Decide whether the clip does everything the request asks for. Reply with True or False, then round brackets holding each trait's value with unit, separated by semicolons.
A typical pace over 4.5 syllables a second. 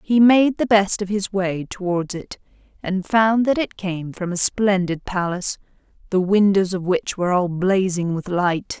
False (4.4 syllables/s)